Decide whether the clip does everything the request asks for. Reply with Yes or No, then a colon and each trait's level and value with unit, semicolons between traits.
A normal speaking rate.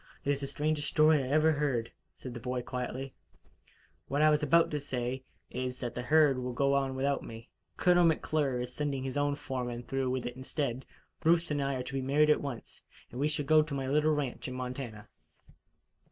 No: fast, 210 wpm